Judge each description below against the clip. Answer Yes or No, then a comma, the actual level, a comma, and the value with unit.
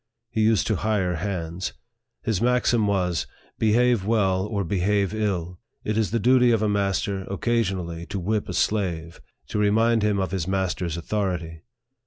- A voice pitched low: Yes, low, 100 Hz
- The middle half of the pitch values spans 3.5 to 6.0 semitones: No, average, 3.1 semitones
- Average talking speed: Yes, average, 160 wpm